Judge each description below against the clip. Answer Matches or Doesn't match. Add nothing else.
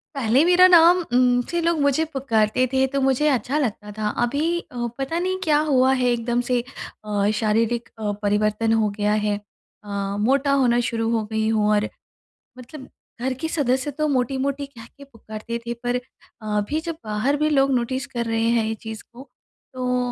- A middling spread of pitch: Matches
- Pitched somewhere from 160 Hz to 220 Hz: Doesn't match